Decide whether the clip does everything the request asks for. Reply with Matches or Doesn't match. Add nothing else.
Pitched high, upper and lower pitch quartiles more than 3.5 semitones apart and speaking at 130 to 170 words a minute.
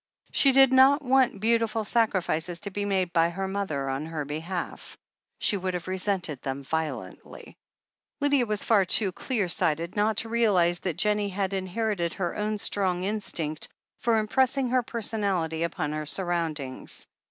Matches